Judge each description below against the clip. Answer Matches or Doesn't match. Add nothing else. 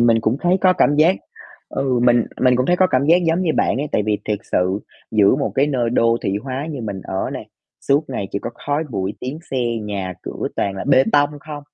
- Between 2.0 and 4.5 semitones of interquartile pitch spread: Doesn't match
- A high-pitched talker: Doesn't match